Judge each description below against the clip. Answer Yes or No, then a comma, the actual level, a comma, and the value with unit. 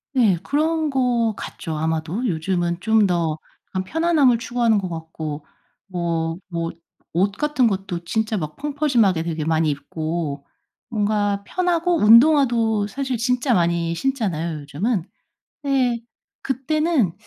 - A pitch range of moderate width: No, wide, 7.4 semitones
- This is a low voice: No, high, 205 Hz